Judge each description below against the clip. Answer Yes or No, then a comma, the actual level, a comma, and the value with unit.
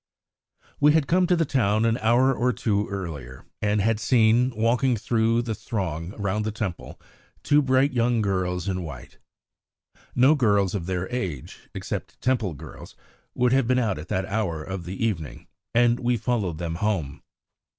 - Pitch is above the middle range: No, low, 110 Hz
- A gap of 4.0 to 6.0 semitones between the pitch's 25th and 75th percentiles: Yes, average, 4.8 semitones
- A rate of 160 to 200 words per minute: Yes, average, 170 wpm